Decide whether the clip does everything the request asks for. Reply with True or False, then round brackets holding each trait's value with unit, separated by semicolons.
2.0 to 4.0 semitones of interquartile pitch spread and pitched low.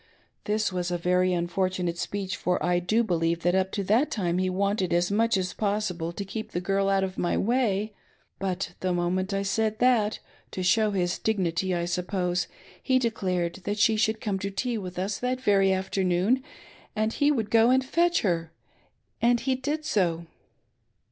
False (3.4 semitones; 195 Hz)